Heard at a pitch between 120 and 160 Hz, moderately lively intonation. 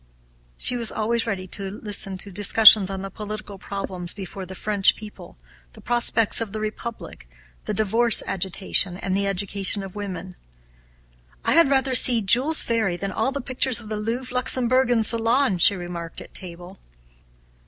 No: high, 210 Hz; average, 3.4 semitones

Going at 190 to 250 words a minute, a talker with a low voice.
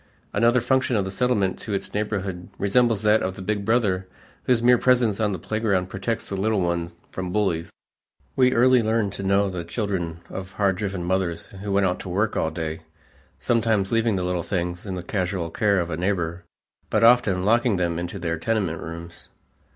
Yes: average, 195 wpm; low, 100 Hz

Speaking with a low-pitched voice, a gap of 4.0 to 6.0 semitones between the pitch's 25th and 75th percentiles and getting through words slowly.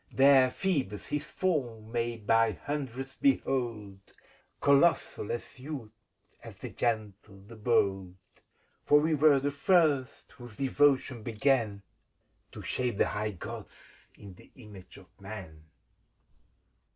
Yes: low, 120 Hz; average, 5.0 semitones; slow, 125 wpm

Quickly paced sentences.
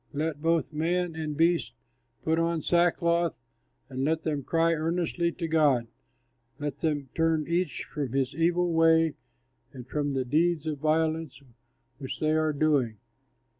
No: average, 145 wpm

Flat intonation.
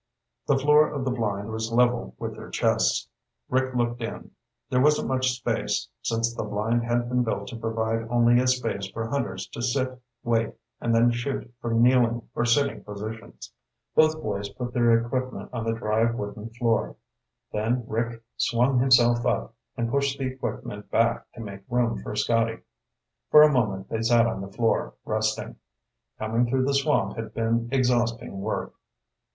Yes: narrow, 1.9 semitones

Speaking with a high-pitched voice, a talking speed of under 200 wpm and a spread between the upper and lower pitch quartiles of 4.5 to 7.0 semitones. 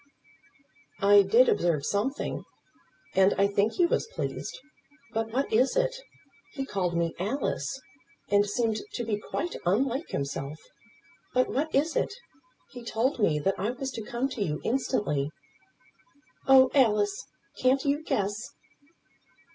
Yes: high, 225 Hz; average, 140 wpm; average, 5.0 semitones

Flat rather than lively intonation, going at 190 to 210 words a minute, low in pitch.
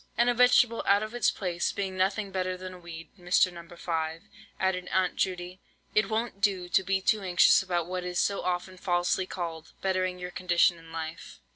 No: narrow, 1.8 semitones; average, 195 wpm; medium, 185 Hz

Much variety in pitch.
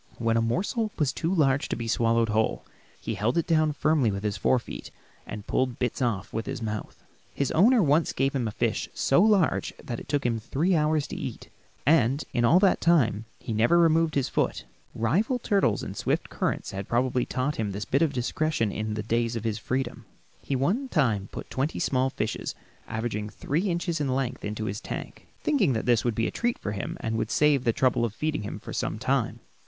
Yes: wide, 5.8 semitones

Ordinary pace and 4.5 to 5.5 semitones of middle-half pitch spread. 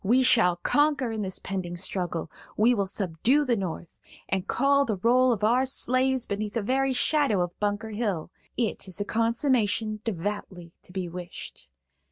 Yes: average, 170 wpm; average, 5.0 semitones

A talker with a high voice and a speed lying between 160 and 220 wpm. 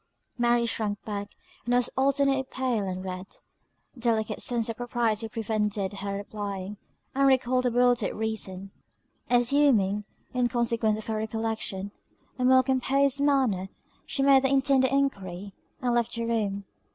No: high, 230 Hz; average, 145 wpm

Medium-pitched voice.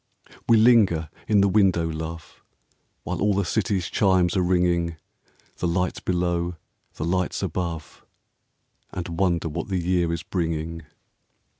No: very low, 90 Hz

